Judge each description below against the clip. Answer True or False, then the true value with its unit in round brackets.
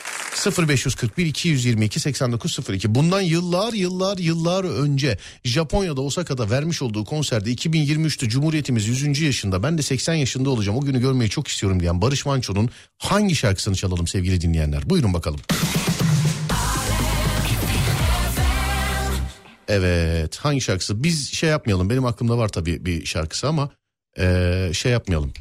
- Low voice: True (125 Hz)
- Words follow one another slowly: False (125 wpm)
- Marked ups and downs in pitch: True (8.0 semitones)